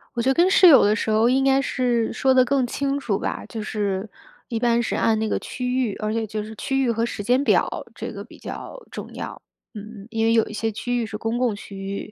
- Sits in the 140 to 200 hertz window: No, high, 230 Hz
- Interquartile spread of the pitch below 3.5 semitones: Yes, average, 2.9 semitones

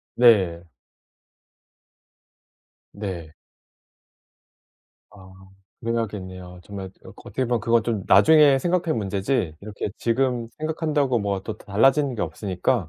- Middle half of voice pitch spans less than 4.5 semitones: No, wide, 5.4 semitones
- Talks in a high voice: No, low, 110 Hz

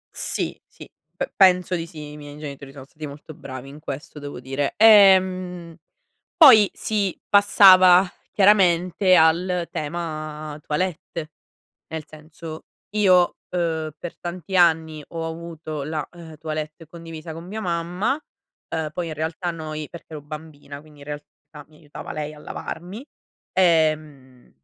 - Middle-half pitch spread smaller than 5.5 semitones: Yes, average, 2.8 semitones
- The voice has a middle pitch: Yes, medium, 160 Hz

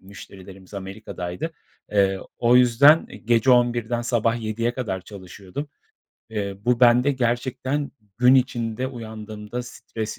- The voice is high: No, low, 115 Hz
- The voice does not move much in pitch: No, average, 3.2 semitones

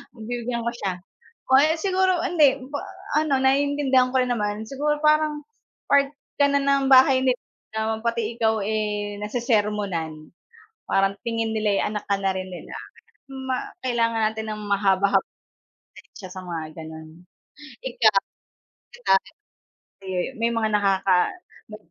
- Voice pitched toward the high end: Yes, high, 225 Hz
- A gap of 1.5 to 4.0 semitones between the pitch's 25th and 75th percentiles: No, average, 4.7 semitones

